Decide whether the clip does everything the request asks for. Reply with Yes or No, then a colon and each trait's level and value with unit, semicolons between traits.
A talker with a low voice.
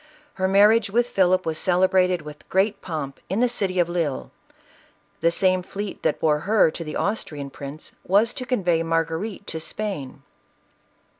No: medium, 185 Hz